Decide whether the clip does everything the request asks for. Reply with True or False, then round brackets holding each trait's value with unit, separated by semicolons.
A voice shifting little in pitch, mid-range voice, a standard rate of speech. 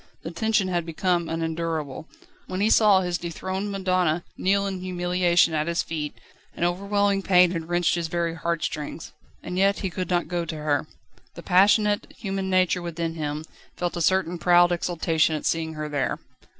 True (2.3 semitones; 175 Hz; 175 wpm)